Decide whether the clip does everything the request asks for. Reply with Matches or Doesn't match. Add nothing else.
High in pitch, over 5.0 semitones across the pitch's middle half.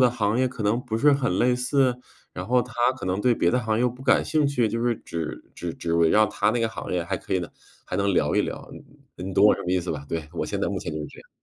Doesn't match